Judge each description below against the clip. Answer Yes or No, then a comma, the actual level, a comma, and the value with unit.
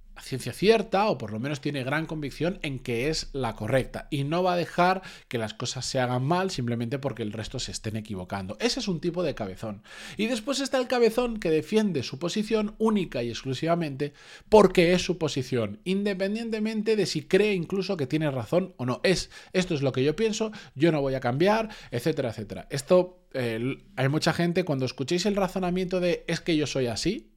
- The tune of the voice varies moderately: No, wide, 6.6 semitones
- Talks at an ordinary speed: No, fast, 205 wpm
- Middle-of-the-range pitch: Yes, medium, 160 Hz